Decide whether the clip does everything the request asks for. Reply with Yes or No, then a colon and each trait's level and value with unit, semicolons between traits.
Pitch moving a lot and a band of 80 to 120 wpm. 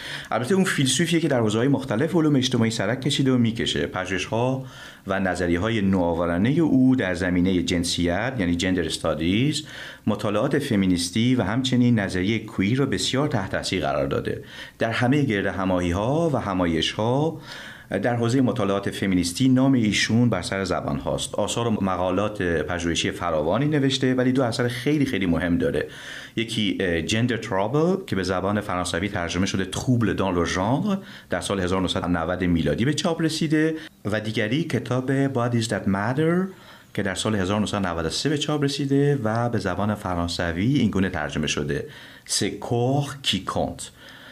No: wide, 6.1 semitones; average, 150 wpm